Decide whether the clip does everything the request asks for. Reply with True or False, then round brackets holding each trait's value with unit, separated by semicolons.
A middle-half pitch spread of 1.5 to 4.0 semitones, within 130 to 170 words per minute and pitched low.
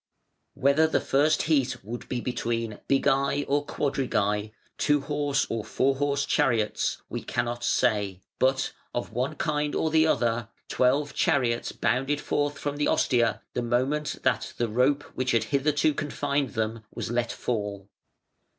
True (3.6 semitones; 150 wpm; 130 Hz)